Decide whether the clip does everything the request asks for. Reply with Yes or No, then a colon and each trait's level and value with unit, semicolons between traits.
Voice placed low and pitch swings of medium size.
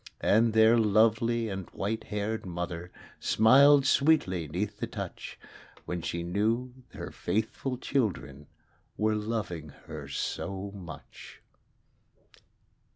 Yes: low, 105 Hz; average, 4.2 semitones